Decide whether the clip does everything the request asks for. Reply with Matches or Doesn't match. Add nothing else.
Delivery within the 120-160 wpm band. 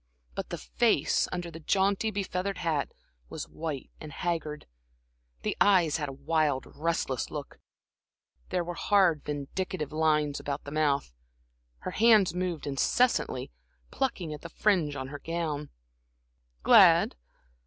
Matches